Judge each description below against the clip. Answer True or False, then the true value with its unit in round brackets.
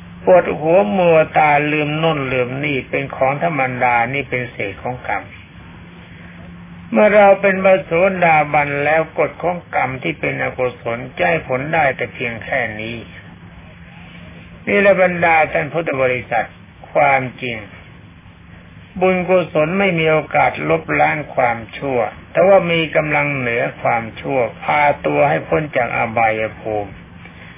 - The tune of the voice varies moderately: False (8.1 semitones)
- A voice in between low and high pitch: False (130 Hz)